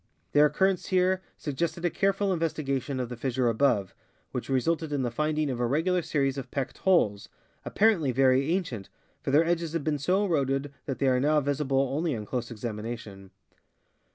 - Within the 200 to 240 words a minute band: No, average, 185 wpm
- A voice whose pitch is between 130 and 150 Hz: Yes, medium, 140 Hz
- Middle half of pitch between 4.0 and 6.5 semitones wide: Yes, average, 4.7 semitones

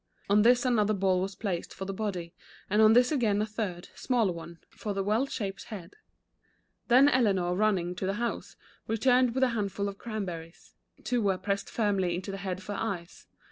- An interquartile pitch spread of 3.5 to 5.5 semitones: No, average, 3.1 semitones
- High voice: Yes, high, 200 Hz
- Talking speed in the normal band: No, fast, 220 wpm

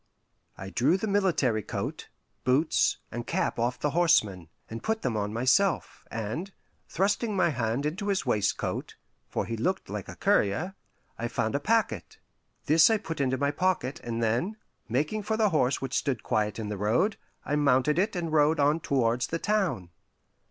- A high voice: No, medium, 140 Hz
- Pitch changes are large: Yes, wide, 8.2 semitones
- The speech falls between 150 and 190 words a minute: Yes, average, 175 wpm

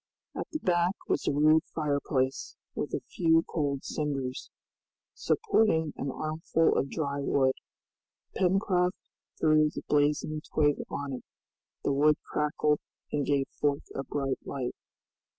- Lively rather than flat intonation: No, narrow, 2.4 semitones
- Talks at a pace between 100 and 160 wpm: Yes, slow, 135 wpm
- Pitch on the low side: No, medium, 150 Hz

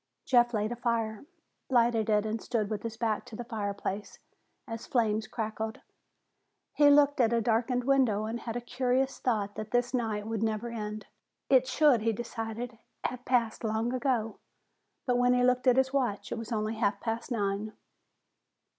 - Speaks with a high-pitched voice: Yes, high, 230 Hz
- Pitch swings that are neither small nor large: No, narrow, 2.3 semitones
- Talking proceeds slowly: No, average, 175 wpm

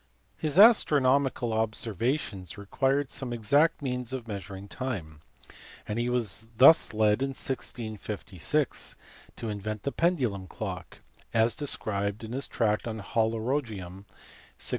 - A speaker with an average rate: No, slow, 120 wpm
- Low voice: Yes, low, 115 Hz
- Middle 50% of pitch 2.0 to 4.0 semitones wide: No, average, 4.4 semitones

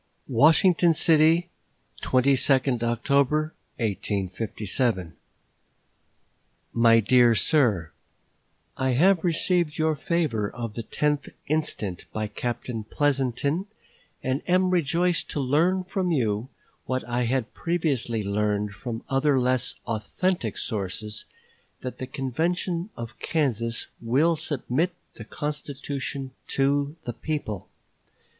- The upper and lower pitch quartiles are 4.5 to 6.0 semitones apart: Yes, wide, 5.4 semitones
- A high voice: No, low, 130 Hz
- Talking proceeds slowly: Yes, slow, 105 wpm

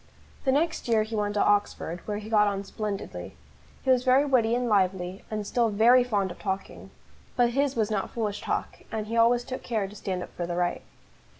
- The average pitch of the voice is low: No, high, 215 Hz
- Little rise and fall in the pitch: No, average, 3.4 semitones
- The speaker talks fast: Yes, fast, 215 wpm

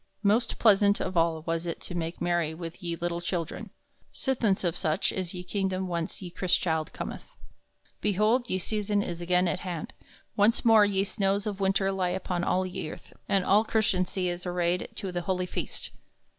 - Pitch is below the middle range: No, medium, 185 Hz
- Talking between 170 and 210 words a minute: Yes, average, 185 wpm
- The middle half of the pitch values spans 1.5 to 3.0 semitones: Yes, narrow, 2.5 semitones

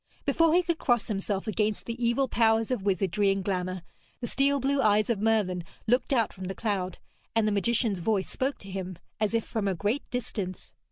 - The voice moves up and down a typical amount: Yes, average, 3.5 semitones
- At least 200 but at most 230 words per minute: Yes, fast, 205 wpm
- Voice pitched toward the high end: Yes, high, 215 Hz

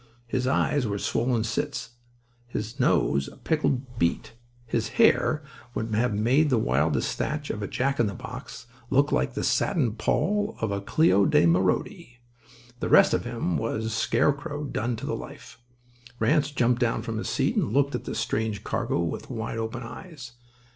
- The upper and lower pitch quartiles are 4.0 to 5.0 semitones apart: Yes, average, 4.4 semitones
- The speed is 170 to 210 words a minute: Yes, average, 175 wpm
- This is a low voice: Yes, low, 120 Hz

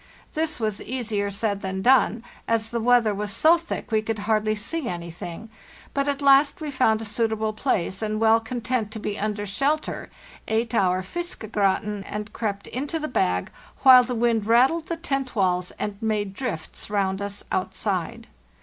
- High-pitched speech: Yes, high, 220 Hz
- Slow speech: No, average, 170 wpm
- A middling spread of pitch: Yes, average, 3.8 semitones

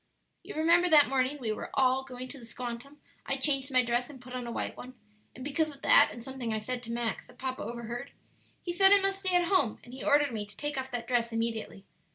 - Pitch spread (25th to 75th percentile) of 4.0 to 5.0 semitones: No, average, 3.5 semitones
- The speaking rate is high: Yes, fast, 250 wpm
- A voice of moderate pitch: No, very high, 255 Hz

